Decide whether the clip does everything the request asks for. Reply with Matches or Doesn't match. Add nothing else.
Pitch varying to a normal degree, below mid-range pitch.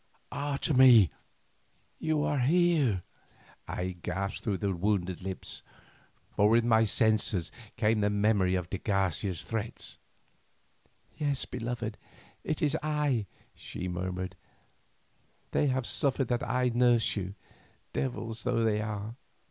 Matches